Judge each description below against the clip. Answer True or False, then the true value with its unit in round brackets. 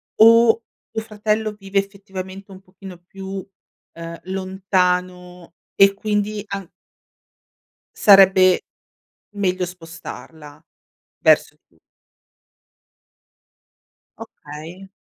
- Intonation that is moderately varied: False (1.8 semitones)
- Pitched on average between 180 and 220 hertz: True (190 Hz)